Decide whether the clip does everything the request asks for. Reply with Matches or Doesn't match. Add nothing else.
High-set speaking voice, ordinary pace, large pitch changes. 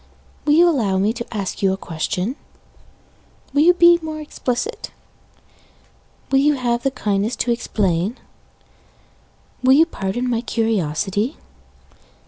Doesn't match